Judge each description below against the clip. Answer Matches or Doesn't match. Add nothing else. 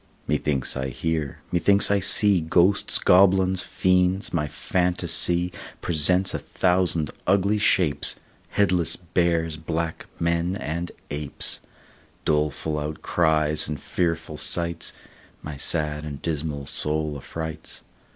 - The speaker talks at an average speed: Doesn't match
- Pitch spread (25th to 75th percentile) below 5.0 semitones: Matches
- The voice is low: Matches